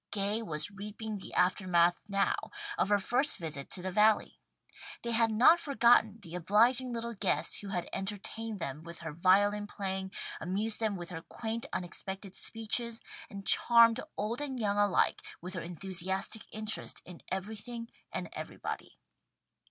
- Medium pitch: No, high, 205 Hz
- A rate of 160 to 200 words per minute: No, average, 150 wpm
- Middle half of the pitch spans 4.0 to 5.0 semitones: No, average, 3.4 semitones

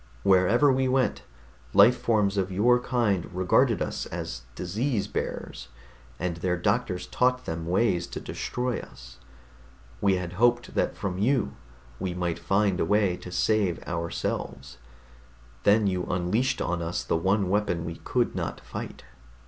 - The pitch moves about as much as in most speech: Yes, average, 4.7 semitones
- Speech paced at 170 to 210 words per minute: No, average, 150 wpm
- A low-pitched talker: Yes, very low, 95 Hz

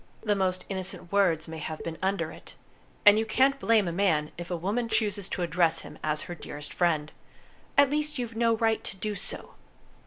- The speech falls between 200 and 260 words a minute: Yes, fast, 205 wpm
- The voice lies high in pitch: Yes, high, 195 Hz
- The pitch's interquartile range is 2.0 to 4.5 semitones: No, average, 4.9 semitones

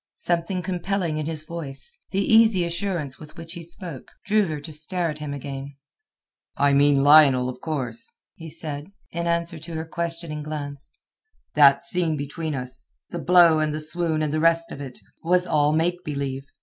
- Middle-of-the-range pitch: Yes, medium, 155 Hz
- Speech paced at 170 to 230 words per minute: Yes, average, 175 wpm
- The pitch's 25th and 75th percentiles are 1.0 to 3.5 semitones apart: Yes, average, 2.9 semitones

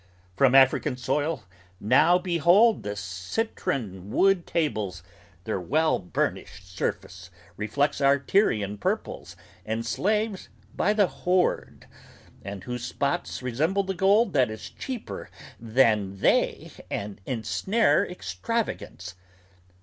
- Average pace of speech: No, slow, 110 wpm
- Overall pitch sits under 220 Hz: Yes, low, 135 Hz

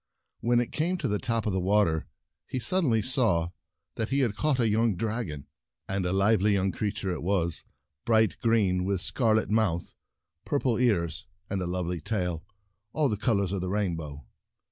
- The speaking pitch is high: No, low, 105 Hz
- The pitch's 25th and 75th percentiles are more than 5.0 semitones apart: No, average, 4.1 semitones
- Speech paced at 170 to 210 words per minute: Yes, average, 190 wpm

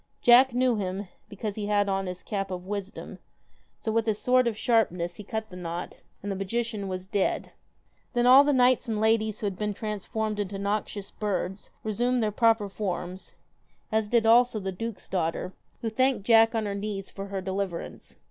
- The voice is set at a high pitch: Yes, high, 210 Hz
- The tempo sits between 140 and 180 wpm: No, average, 190 wpm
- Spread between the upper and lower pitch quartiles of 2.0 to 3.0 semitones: Yes, average, 2.7 semitones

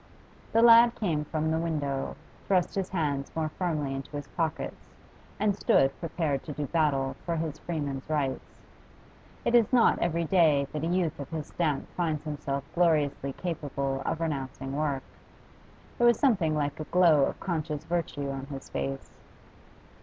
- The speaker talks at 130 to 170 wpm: Yes, average, 160 wpm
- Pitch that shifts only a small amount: No, average, 3.5 semitones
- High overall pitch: No, medium, 155 Hz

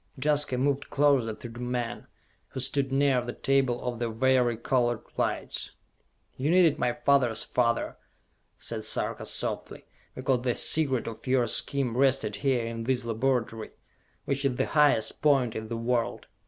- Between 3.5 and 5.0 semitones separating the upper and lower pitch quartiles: No, narrow, 2.6 semitones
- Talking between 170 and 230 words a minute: No, average, 155 wpm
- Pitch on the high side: No, low, 125 Hz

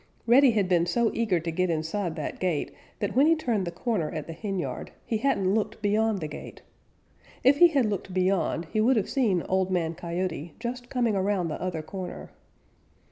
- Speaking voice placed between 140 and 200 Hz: Yes, high, 190 Hz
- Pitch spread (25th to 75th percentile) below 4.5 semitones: No, average, 4.8 semitones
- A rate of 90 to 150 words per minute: No, average, 195 wpm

